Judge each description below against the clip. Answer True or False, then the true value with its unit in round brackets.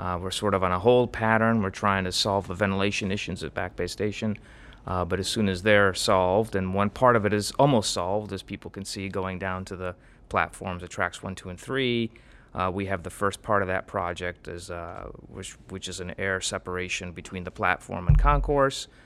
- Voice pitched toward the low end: True (95 Hz)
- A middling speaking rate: False (225 wpm)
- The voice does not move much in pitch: True (2.3 semitones)